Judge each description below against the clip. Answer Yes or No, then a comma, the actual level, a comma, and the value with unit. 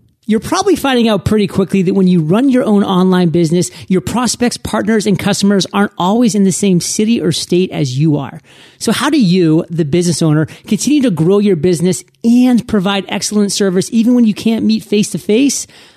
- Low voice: No, high, 200 Hz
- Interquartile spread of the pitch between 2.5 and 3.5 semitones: No, average, 3.9 semitones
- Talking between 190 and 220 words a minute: Yes, fast, 205 wpm